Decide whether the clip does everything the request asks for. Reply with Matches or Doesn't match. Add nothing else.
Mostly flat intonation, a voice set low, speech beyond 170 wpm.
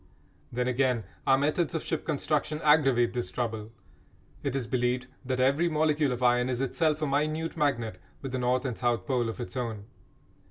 Doesn't match